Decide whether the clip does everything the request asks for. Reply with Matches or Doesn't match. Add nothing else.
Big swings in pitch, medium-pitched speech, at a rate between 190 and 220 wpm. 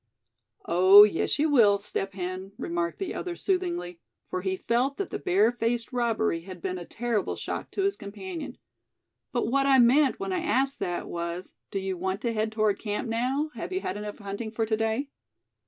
Doesn't match